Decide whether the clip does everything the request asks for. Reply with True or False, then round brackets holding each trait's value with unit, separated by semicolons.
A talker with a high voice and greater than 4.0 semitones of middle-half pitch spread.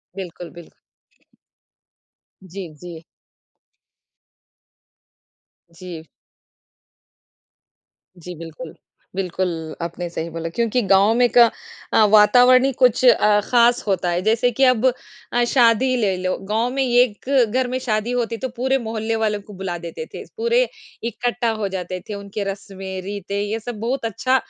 True (215 Hz; 4.6 semitones)